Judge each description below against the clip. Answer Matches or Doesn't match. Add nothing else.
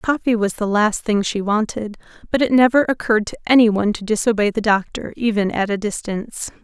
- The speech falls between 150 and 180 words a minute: Doesn't match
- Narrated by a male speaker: Doesn't match